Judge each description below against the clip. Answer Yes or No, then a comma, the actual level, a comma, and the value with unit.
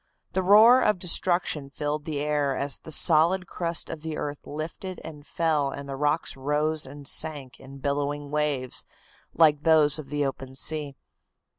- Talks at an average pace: Yes, average, 165 wpm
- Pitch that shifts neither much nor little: No, narrow, 2.2 semitones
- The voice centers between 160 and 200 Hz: No, medium, 150 Hz